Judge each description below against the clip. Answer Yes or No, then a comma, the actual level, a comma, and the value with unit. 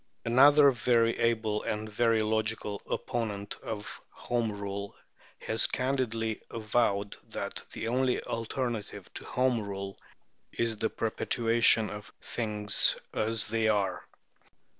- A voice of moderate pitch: No, low, 110 Hz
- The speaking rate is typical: No, slow, 115 wpm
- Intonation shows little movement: Yes, narrow, 2.0 semitones